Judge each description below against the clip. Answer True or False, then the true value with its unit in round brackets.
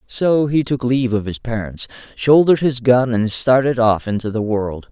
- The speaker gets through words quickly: False (195 wpm)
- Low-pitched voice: True (120 Hz)